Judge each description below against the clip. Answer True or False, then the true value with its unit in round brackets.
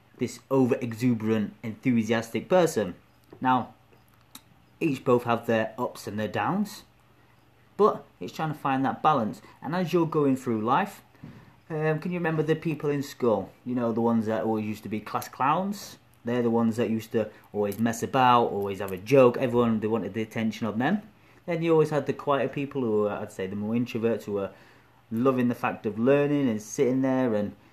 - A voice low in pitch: True (120 Hz)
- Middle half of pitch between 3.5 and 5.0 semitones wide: True (3.9 semitones)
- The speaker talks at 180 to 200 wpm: True (195 wpm)